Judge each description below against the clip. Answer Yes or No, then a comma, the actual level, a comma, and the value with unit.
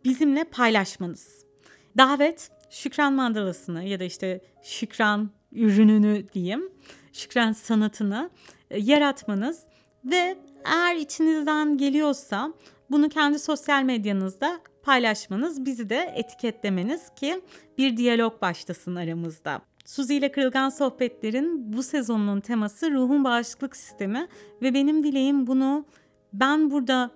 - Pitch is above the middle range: Yes, very high, 260 Hz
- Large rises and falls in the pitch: Yes, wide, 5.7 semitones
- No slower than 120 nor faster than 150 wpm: No, average, 105 wpm